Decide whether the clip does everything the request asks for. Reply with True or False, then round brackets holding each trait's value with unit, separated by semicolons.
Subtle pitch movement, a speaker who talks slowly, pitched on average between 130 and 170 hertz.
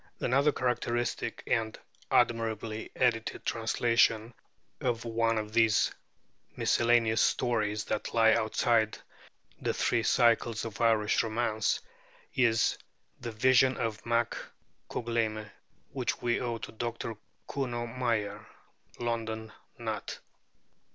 False (1.3 semitones; 105 wpm; 115 Hz)